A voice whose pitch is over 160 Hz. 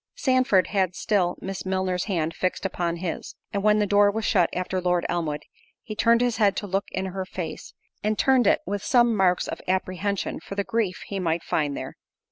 Yes: high, 190 Hz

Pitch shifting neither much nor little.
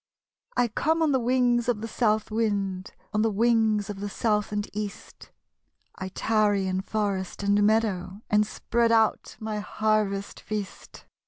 No: narrow, 2.0 semitones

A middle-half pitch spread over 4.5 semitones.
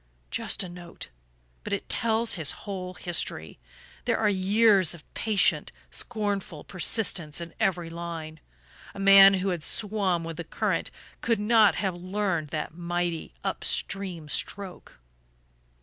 No: average, 3.1 semitones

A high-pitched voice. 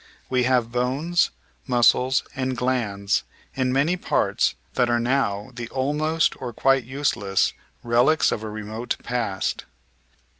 No: low, 125 Hz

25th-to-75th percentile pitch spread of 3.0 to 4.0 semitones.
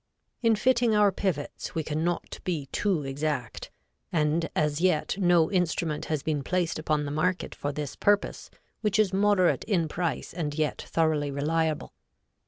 Yes: average, 3.6 semitones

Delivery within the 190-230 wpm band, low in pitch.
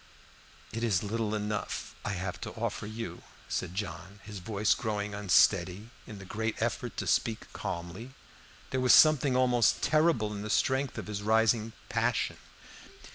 No: average, 155 wpm; low, 105 Hz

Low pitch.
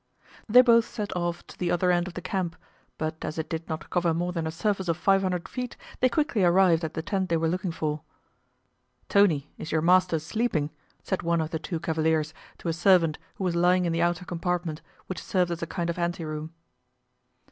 No: medium, 175 Hz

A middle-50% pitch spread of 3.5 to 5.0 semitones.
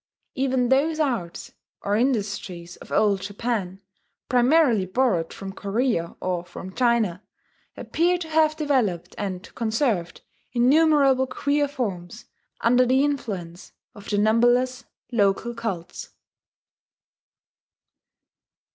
No: wide, 5.5 semitones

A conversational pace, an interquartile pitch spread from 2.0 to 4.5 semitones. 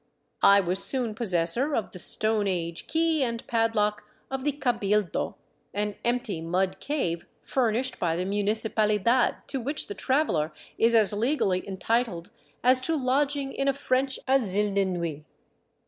No: average, 155 wpm; average, 5.2 semitones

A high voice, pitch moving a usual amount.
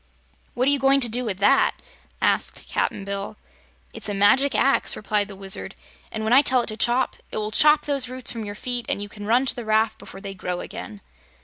Yes: high, 220 Hz; average, 3.8 semitones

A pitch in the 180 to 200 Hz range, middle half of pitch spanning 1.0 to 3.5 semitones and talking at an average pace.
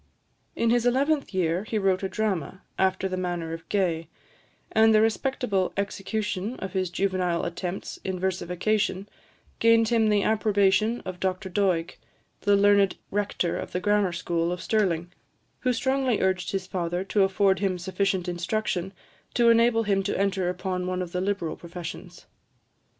Yes: high, 190 Hz; average, 2.8 semitones; average, 155 wpm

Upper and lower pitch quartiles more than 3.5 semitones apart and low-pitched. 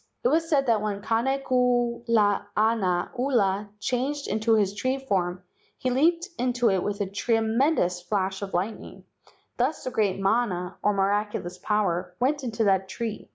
No: average, 4.2 semitones; high, 220 Hz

